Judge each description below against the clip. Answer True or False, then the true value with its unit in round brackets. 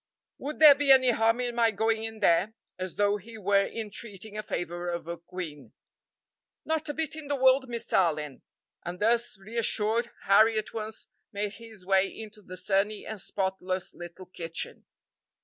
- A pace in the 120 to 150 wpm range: False (170 wpm)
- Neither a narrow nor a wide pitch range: True (3.8 semitones)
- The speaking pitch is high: True (215 Hz)